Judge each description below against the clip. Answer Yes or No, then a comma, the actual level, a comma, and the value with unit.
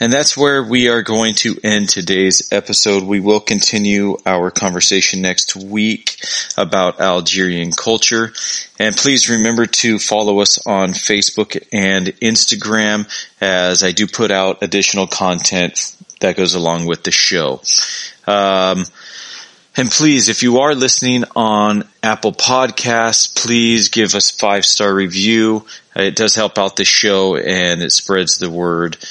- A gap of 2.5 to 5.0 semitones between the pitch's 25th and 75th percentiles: Yes, average, 3.0 semitones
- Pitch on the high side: No, low, 100 Hz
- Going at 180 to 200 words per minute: No, average, 145 wpm